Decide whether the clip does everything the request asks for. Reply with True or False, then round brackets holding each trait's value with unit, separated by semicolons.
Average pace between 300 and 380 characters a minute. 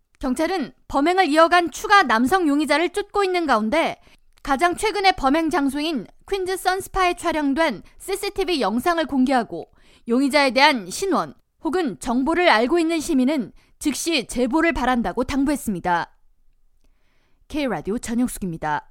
True (310 characters per minute)